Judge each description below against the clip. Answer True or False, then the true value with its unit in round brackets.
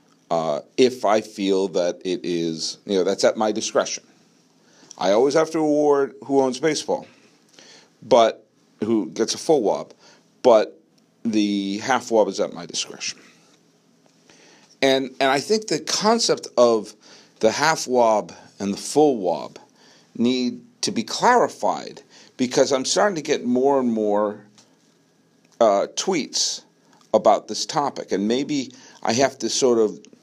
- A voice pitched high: False (125 Hz)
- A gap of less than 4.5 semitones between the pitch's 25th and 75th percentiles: False (5.6 semitones)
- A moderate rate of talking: True (145 wpm)